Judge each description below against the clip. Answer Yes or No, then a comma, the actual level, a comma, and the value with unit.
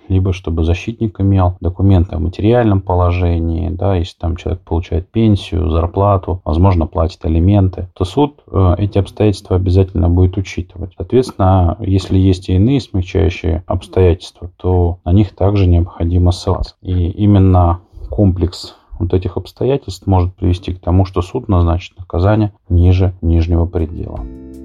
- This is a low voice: Yes, very low, 90 Hz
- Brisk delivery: No, average, 135 wpm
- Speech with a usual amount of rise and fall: No, narrow, 2.0 semitones